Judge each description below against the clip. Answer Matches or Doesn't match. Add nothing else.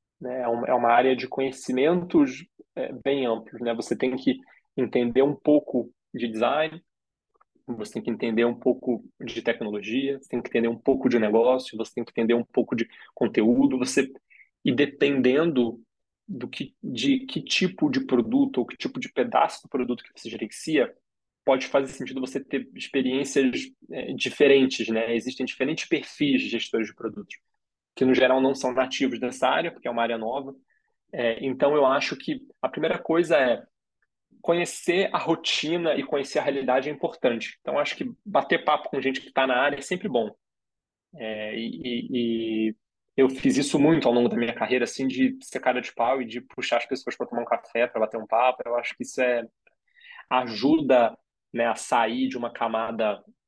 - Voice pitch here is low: Matches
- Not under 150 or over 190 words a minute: Matches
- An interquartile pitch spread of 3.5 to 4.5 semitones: Doesn't match